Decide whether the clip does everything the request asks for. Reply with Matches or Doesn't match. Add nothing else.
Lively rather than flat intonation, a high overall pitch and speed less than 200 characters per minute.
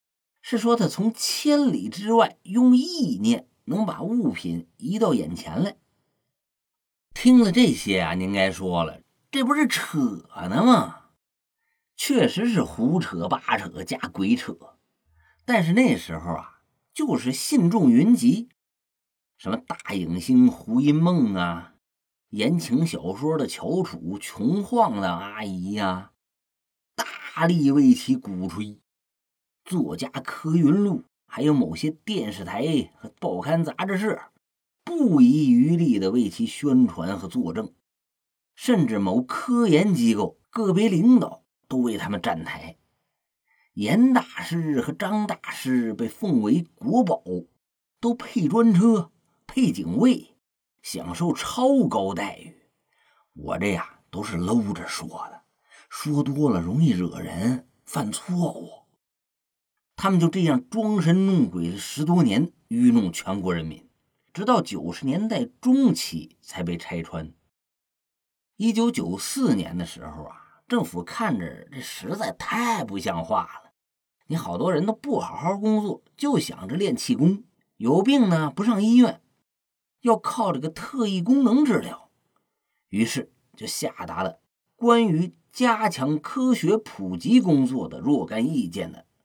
Matches